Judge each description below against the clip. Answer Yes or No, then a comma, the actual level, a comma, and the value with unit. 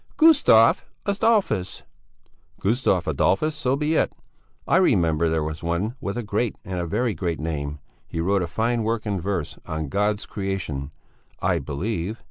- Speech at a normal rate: Yes, average, 150 wpm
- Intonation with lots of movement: Yes, wide, 5.8 semitones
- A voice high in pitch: No, low, 100 Hz